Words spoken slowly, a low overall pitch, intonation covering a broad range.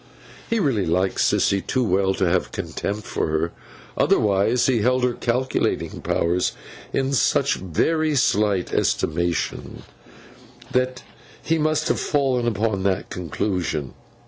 Yes: slow, 130 wpm; low, 105 Hz; wide, 5.7 semitones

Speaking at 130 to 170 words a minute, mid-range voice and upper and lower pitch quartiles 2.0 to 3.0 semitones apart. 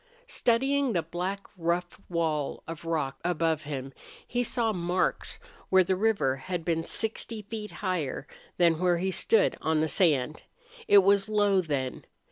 No: average, 150 wpm; medium, 180 Hz; average, 4.1 semitones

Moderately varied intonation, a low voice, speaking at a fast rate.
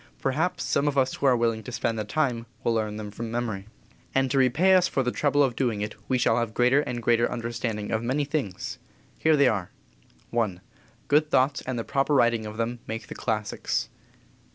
Yes: average, 3.5 semitones; low, 120 Hz; fast, 210 wpm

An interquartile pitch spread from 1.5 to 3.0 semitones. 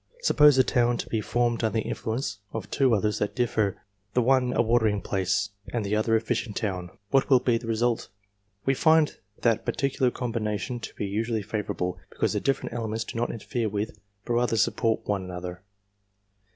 Yes: average, 2.7 semitones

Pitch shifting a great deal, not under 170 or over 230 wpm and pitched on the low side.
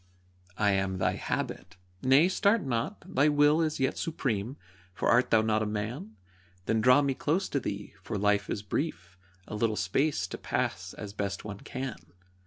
Yes: wide, 5.7 semitones; average, 180 wpm; low, 110 Hz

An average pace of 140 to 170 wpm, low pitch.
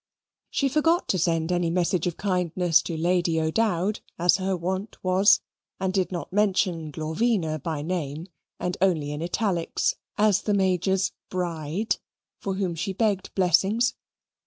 No: average, 145 wpm; medium, 180 Hz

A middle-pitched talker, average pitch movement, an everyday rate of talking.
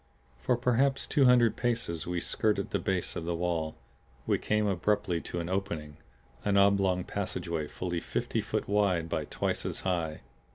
No: very low, 95 Hz; average, 3.7 semitones; average, 165 wpm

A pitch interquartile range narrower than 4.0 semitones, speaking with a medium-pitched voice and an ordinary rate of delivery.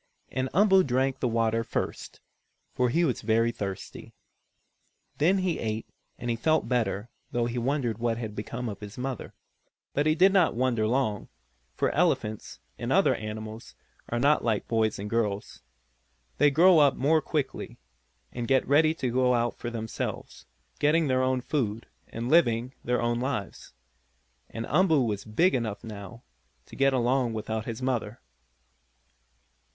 No: average, 3.5 semitones; low, 120 Hz; average, 155 wpm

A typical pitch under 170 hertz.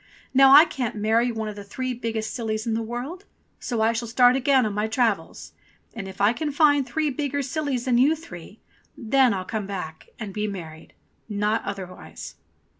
No: high, 230 Hz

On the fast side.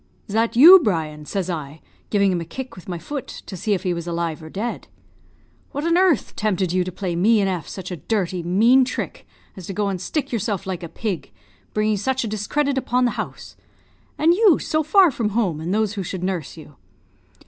Yes: fast, 220 wpm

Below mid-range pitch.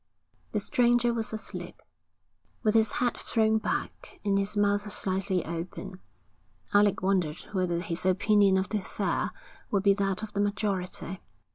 No: high, 200 Hz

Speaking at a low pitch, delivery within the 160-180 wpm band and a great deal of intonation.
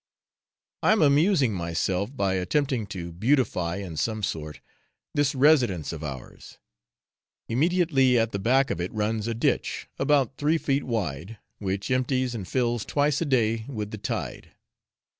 No: low, 115 Hz; average, 150 wpm; wide, 6.2 semitones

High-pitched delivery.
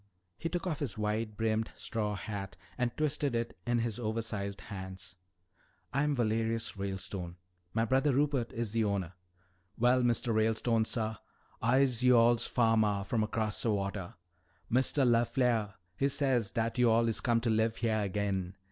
No: low, 115 Hz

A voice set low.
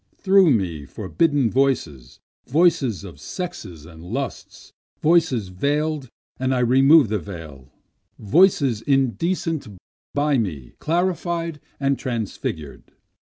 Yes: low, 130 Hz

